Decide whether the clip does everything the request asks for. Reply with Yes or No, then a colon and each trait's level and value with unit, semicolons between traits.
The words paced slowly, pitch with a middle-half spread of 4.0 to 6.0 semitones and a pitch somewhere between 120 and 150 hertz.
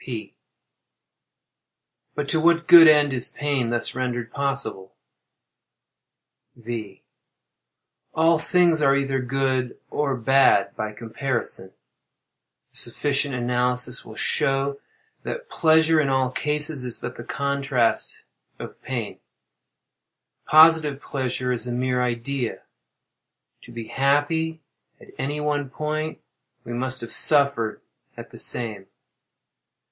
No: slow, 115 wpm; average, 3.3 semitones; low, 135 Hz